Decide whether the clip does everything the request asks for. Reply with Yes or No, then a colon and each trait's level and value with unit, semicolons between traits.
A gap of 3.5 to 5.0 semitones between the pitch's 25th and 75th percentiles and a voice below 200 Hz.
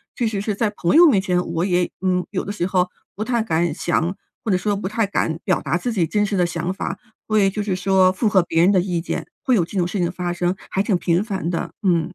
No: average, 2.7 semitones; medium, 185 Hz